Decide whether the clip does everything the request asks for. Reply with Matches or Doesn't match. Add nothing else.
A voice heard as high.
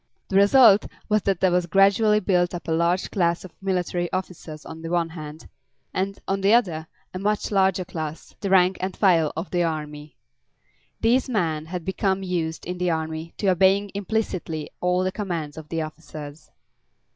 Doesn't match